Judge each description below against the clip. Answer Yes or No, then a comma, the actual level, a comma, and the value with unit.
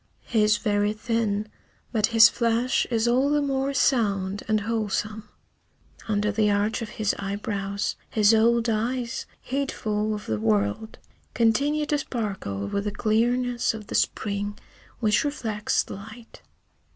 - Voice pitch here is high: Yes, high, 220 Hz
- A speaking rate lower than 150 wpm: Yes, average, 140 wpm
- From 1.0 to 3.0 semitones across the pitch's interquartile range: Yes, narrow, 2.4 semitones